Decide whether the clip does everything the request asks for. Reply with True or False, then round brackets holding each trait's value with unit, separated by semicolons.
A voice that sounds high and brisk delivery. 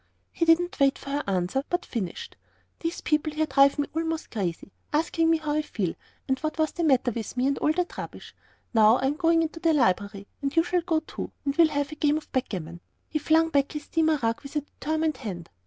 True (295 Hz; 230 wpm)